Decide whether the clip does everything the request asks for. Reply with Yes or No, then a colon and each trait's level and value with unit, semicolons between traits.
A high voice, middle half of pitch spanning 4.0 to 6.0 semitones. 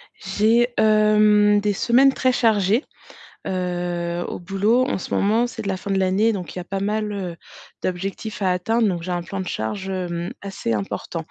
No: high, 195 Hz; average, 3.0 semitones